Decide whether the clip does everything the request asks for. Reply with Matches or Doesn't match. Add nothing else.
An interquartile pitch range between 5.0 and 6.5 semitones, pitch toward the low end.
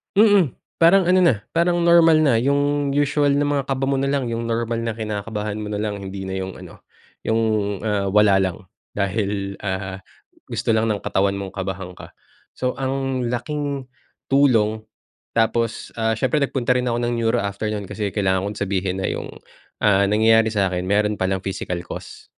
Matches